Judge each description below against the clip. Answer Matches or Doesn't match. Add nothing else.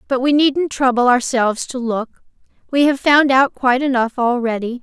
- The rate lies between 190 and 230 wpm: Doesn't match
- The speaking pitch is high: Matches